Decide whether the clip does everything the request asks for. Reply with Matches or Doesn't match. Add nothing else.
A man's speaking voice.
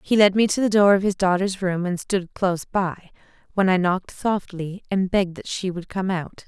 Doesn't match